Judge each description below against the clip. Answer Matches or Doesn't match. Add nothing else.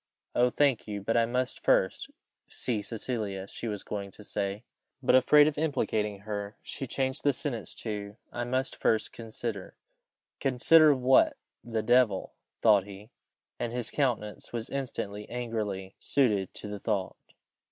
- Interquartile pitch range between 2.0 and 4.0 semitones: Matches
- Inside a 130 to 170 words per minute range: Matches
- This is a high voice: Doesn't match